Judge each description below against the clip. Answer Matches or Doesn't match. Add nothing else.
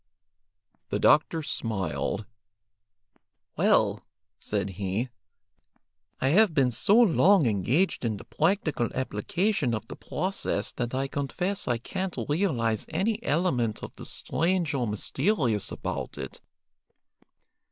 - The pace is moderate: Doesn't match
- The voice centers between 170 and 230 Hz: Doesn't match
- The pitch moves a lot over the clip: Matches